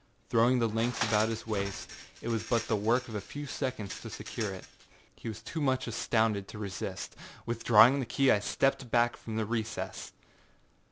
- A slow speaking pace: No, average, 185 wpm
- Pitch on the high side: No, low, 115 Hz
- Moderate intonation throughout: No, narrow, 2.3 semitones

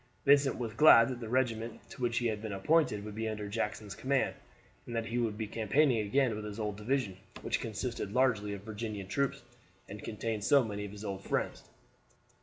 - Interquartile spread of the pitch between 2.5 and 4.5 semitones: Yes, average, 3.1 semitones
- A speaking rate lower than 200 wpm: No, fast, 205 wpm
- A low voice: Yes, low, 110 Hz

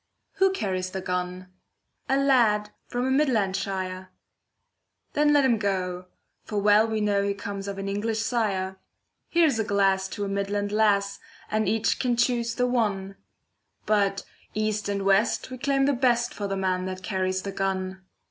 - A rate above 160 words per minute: Yes, average, 170 wpm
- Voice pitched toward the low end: No, high, 205 Hz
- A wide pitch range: No, average, 3.3 semitones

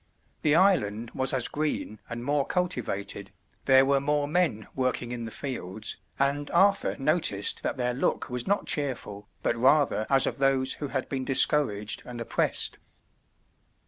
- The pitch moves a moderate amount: Yes, average, 3.8 semitones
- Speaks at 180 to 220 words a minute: No, average, 155 wpm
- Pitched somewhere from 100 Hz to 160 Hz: Yes, low, 135 Hz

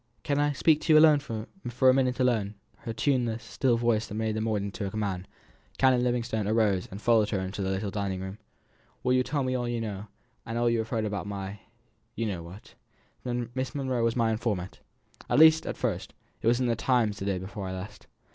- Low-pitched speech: Yes, low, 115 Hz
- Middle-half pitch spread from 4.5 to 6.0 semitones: No, average, 3.8 semitones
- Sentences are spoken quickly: Yes, fast, 215 wpm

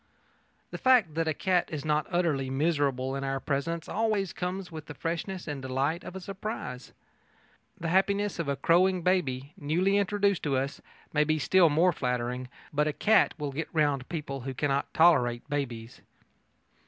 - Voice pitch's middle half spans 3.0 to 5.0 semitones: Yes, average, 4.7 semitones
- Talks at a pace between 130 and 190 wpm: Yes, average, 170 wpm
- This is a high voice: No, medium, 155 Hz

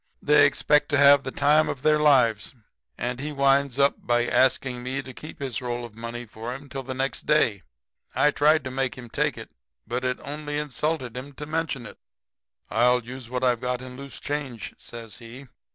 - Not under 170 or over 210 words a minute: Yes, average, 200 wpm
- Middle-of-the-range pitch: No, low, 130 Hz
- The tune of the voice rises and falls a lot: No, average, 2.8 semitones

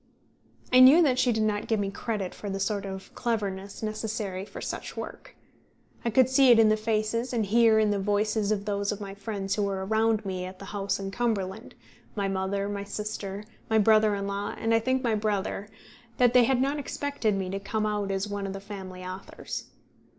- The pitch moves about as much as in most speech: No, narrow, 2.2 semitones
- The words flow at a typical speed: No, fast, 210 wpm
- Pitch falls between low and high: No, high, 210 Hz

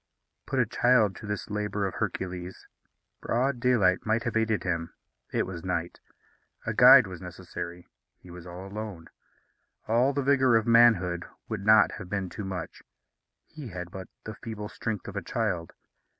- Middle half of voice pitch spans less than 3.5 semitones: No, average, 4.3 semitones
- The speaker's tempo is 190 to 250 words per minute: No, average, 165 wpm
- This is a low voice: Yes, low, 105 Hz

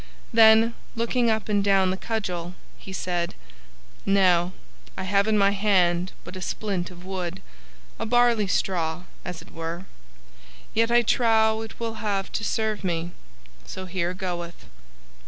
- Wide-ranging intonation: No, average, 3.7 semitones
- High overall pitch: Yes, high, 195 Hz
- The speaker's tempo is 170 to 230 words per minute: No, average, 150 wpm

